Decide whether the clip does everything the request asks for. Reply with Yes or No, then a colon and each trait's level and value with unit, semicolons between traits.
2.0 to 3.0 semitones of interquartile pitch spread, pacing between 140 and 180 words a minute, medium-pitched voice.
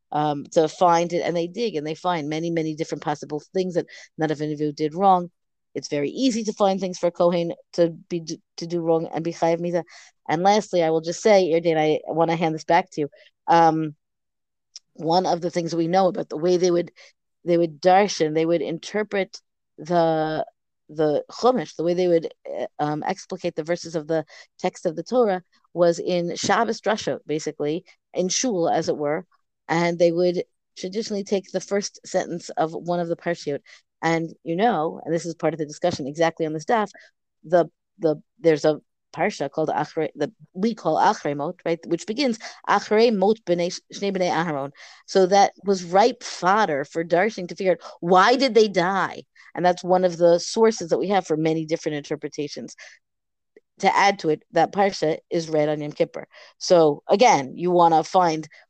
No: average, 2.7 semitones; average, 195 wpm; medium, 170 Hz